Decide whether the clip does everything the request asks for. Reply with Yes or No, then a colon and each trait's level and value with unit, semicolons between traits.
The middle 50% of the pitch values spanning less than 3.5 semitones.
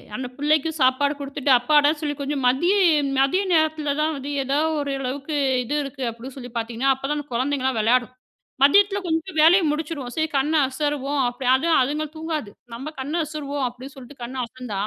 Yes: average, 3.1 semitones